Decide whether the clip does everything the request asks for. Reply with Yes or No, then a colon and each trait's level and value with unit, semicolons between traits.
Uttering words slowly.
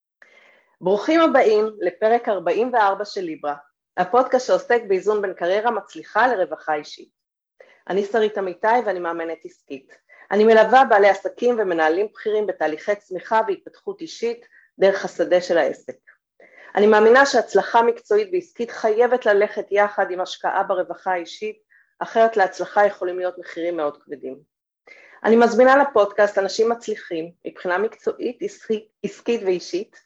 No: average, 125 wpm